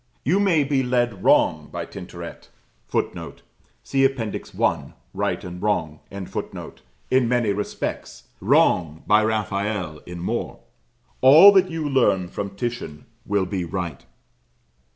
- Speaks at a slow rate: Yes, slow, 125 wpm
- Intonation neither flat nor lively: No, wide, 6.3 semitones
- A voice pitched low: Yes, low, 105 Hz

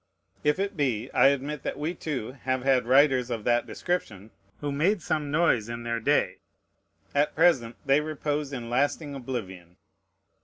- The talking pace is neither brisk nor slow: Yes, average, 160 wpm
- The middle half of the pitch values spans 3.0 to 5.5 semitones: Yes, average, 4.0 semitones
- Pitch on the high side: No, low, 135 Hz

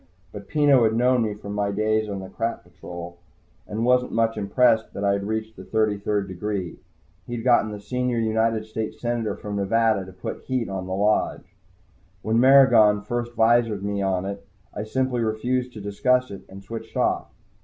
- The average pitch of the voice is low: Yes, low, 110 Hz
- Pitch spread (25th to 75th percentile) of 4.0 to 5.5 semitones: No, average, 2.8 semitones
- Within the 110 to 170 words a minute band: No, average, 185 wpm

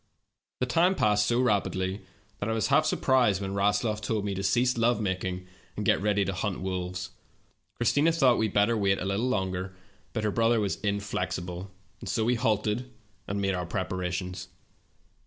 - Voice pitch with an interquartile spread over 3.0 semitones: Yes, average, 3.4 semitones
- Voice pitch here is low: Yes, low, 100 Hz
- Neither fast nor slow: Yes, average, 185 wpm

